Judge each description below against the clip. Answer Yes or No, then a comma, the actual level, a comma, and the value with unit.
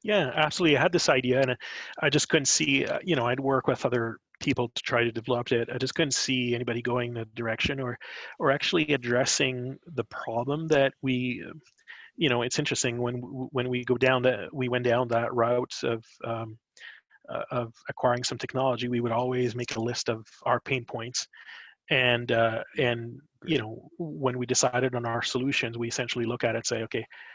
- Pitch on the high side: No, low, 125 Hz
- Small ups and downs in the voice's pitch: Yes, narrow, 1.9 semitones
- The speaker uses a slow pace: No, average, 195 wpm